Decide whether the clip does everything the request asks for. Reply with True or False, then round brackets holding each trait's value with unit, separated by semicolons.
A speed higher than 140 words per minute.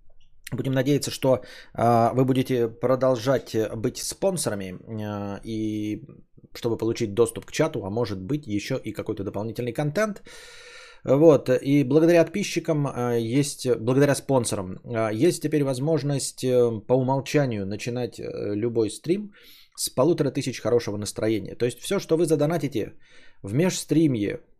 False (120 wpm)